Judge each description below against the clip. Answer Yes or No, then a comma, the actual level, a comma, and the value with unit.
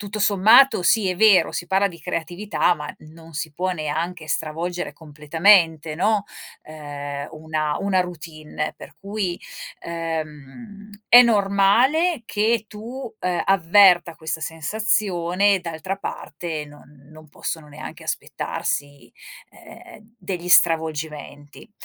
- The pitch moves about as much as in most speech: Yes, average, 4.6 semitones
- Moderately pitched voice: Yes, medium, 175 Hz